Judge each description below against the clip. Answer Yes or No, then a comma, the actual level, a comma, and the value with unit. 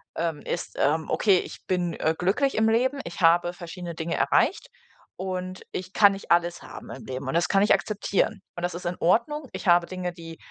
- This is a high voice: No, medium, 180 Hz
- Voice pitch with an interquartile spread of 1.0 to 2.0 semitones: No, average, 2.7 semitones